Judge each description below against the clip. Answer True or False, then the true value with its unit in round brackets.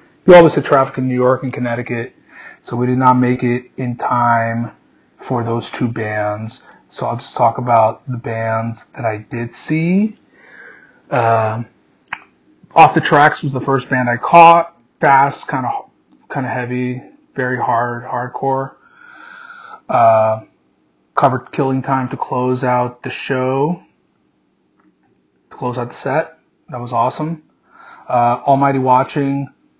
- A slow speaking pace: False (145 wpm)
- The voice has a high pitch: False (125 Hz)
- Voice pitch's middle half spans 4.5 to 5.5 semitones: False (2.8 semitones)